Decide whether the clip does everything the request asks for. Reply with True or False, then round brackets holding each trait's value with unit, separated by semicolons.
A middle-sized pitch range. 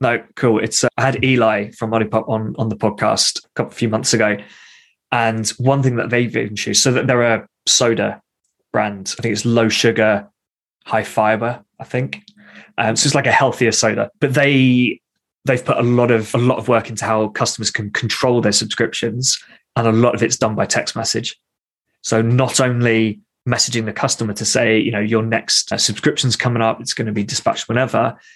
False (2.3 semitones)